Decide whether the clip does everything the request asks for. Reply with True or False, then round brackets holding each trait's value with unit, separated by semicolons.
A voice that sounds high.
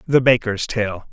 False (115 Hz)